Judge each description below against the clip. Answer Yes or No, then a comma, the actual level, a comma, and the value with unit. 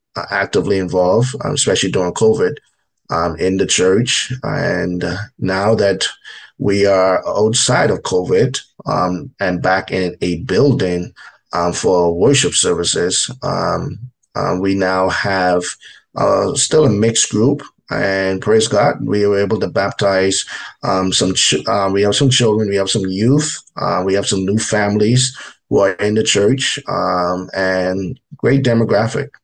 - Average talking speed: Yes, average, 145 wpm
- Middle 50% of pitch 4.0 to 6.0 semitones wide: Yes, average, 4.4 semitones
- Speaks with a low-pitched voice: Yes, low, 100 Hz